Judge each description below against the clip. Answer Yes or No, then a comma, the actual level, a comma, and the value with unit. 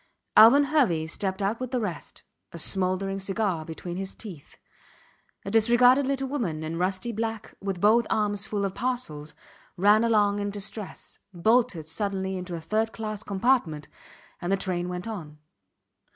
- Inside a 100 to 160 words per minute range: Yes, average, 155 wpm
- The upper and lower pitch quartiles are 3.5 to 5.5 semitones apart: Yes, average, 3.8 semitones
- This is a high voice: Yes, high, 200 Hz